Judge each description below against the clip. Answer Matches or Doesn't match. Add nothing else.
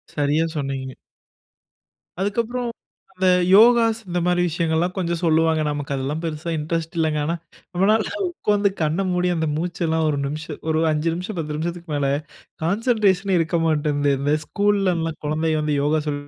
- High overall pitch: Doesn't match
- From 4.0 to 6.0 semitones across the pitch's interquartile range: Doesn't match